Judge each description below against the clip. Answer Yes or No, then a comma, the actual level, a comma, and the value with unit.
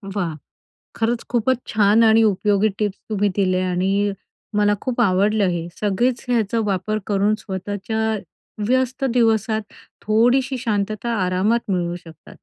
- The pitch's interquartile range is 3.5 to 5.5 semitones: No, average, 2.9 semitones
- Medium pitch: No, high, 210 Hz